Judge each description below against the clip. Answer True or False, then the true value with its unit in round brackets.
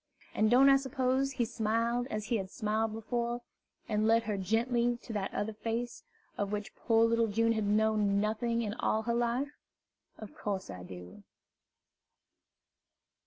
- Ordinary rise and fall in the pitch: False (2.1 semitones)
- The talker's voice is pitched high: True (225 Hz)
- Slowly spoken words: False (160 wpm)